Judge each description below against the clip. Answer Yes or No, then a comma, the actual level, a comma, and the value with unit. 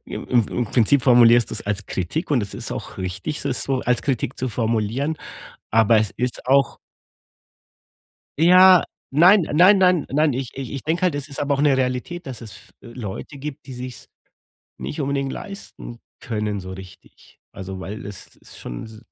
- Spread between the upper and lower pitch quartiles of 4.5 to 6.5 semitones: Yes, average, 4.9 semitones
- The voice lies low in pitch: Yes, low, 125 Hz